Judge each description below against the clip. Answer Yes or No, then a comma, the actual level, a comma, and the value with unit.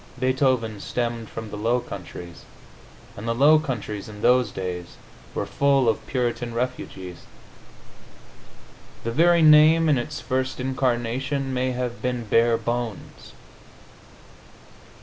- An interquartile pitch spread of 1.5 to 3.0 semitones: Yes, average, 2.7 semitones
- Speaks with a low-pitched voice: Yes, low, 120 Hz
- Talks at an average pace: No, slow, 115 wpm